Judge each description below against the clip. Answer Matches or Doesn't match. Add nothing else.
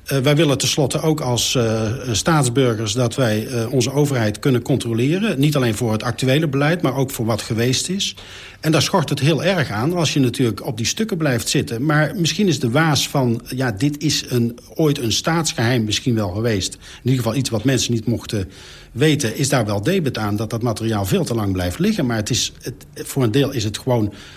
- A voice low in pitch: Matches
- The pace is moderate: Doesn't match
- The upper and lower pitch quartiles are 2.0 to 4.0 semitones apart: Doesn't match